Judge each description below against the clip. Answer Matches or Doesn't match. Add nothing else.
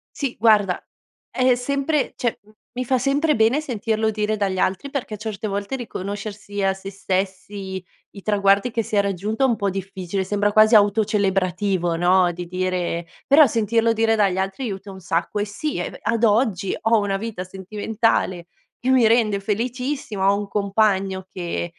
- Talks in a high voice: Matches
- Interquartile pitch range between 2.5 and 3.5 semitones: Matches